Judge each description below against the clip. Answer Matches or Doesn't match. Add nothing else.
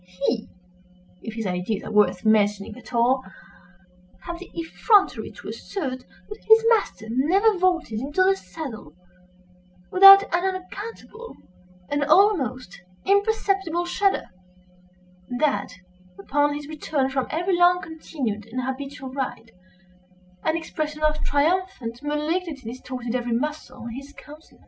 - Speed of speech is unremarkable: Doesn't match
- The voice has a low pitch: Doesn't match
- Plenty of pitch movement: Matches